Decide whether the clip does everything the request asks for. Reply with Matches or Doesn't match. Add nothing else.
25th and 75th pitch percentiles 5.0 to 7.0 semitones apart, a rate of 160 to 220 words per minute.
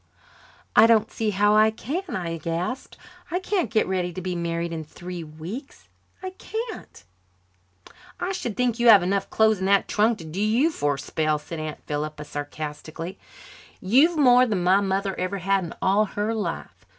Matches